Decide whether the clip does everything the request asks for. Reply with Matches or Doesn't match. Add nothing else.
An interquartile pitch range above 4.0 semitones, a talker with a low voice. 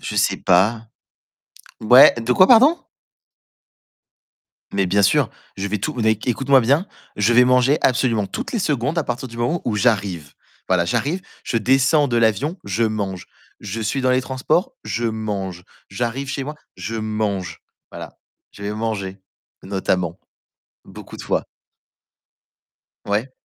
Matches